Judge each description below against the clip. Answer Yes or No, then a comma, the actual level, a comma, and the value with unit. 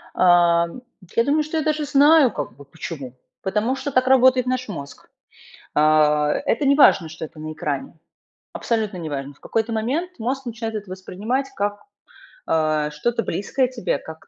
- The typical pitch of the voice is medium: No, high, 220 Hz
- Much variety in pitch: Yes, wide, 8.1 semitones